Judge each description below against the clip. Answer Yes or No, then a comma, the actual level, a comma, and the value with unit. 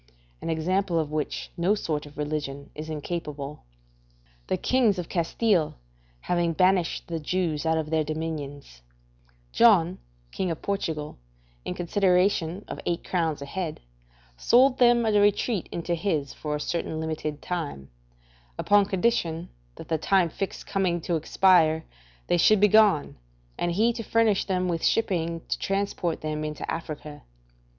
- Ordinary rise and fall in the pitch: Yes, average, 3.8 semitones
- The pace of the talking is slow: No, average, 145 wpm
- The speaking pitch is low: No, medium, 170 Hz